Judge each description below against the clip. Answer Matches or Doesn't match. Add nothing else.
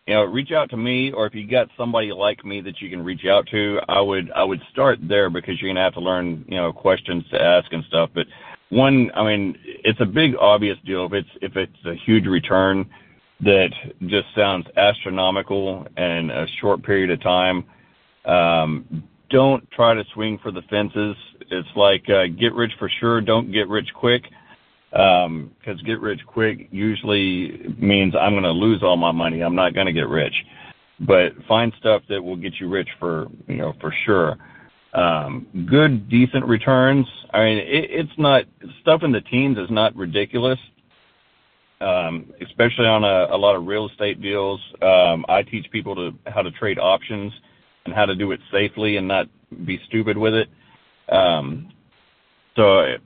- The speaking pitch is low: Matches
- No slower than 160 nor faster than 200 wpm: Matches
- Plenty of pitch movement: Doesn't match